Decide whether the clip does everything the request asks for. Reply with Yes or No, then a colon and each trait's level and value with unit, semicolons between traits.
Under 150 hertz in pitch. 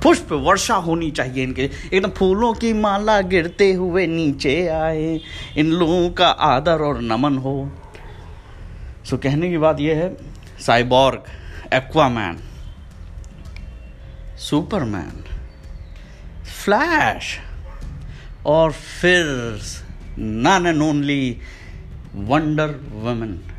Yes: low, 135 Hz